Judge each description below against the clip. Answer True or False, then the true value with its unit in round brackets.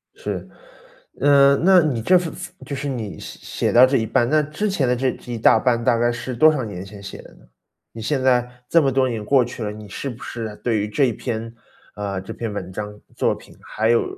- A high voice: False (120 Hz)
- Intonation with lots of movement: False (3.9 semitones)